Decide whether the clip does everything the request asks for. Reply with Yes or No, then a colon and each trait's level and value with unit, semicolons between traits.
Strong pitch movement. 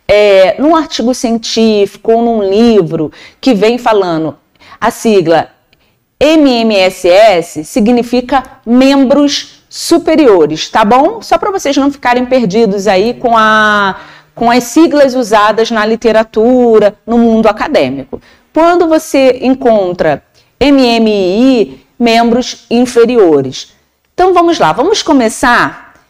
No: average, 4.2 semitones